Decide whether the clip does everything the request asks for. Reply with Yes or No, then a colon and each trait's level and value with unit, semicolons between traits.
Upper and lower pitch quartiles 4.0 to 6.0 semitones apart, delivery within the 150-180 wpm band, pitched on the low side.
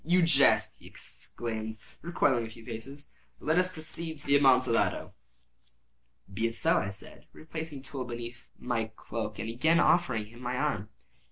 Yes: wide, 5.4 semitones; average, 170 wpm; low, 125 Hz